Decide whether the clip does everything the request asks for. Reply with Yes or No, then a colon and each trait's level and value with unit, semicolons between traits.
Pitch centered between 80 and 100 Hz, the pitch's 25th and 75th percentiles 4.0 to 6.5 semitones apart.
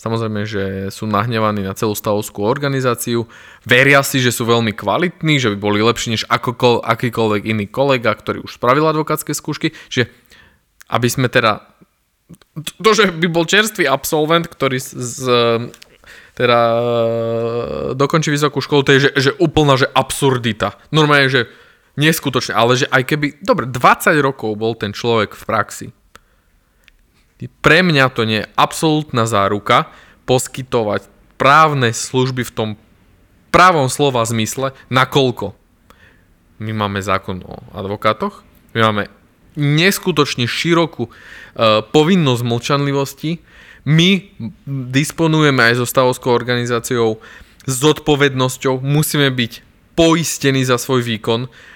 No: low, 125 Hz; average, 4.6 semitones